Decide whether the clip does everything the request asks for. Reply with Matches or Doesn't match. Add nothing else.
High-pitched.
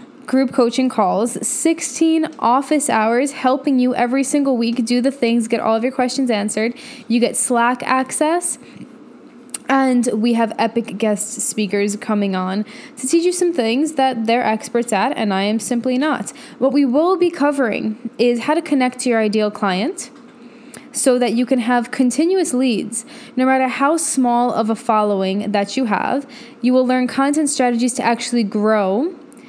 Matches